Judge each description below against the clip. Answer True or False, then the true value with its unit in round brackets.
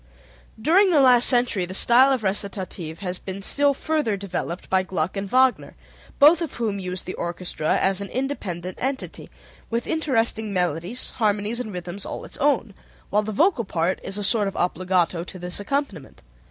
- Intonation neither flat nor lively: False (5.7 semitones)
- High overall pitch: True (205 Hz)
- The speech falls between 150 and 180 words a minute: True (175 wpm)